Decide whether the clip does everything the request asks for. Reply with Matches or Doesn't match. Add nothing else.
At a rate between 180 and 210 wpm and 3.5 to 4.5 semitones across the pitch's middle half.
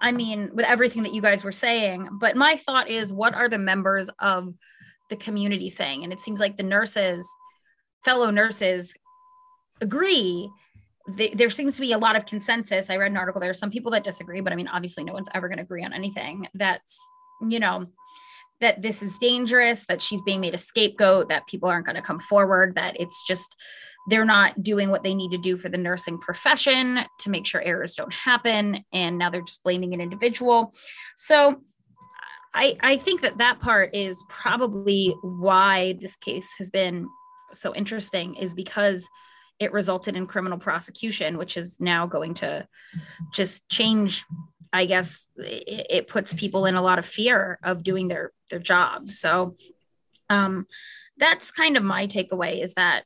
Matches